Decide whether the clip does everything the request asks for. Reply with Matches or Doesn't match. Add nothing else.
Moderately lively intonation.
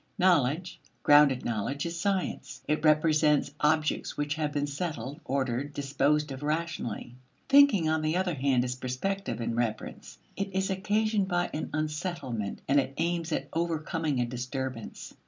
Matches